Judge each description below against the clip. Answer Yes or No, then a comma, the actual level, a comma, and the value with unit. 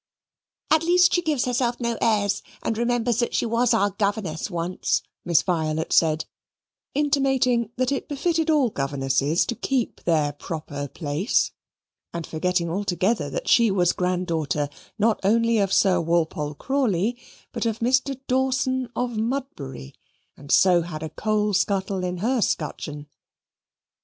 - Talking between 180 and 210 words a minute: No, average, 140 wpm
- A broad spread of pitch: Yes, wide, 6.7 semitones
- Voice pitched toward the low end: No, high, 205 Hz